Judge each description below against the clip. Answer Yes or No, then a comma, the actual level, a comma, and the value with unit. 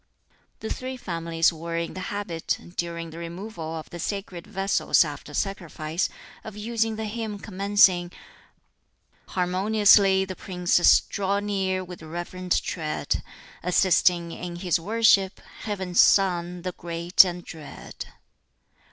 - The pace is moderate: No, slow, 125 wpm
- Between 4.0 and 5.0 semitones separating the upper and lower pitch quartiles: No, average, 2.8 semitones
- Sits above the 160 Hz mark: Yes, medium, 185 Hz